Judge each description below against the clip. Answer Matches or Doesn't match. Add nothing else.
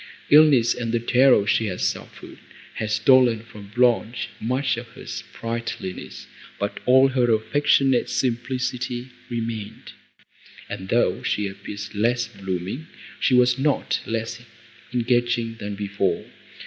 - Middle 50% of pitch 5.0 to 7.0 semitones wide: Doesn't match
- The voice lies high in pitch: Doesn't match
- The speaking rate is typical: Doesn't match